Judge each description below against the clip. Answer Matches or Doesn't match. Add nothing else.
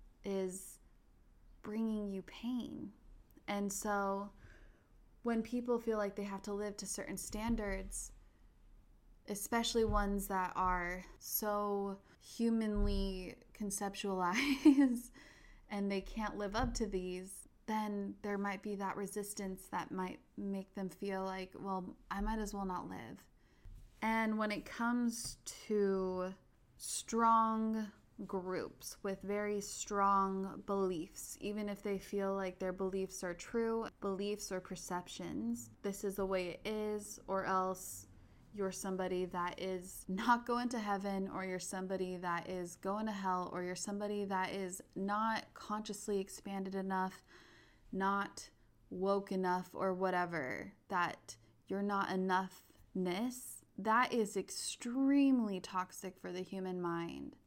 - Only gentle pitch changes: Matches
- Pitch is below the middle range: Doesn't match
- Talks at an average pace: Doesn't match